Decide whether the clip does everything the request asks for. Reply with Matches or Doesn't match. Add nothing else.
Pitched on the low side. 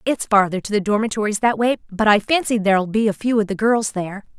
Doesn't match